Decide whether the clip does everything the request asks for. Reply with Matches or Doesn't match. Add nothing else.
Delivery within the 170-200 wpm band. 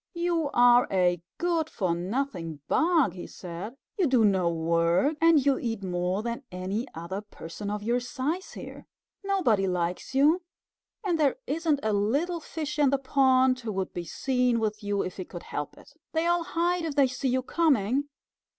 Matches